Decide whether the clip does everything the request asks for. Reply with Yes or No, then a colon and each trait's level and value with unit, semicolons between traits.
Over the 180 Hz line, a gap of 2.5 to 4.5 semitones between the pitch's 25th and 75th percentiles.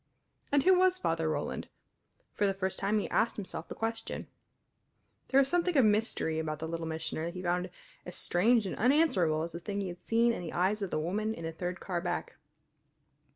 No: high, 190 Hz; average, 5.2 semitones